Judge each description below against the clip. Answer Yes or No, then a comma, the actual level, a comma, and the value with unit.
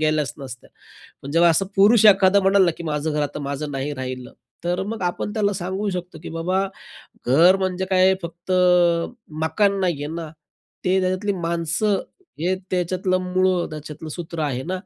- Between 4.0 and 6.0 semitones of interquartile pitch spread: No, average, 3.5 semitones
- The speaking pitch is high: No, medium, 175 Hz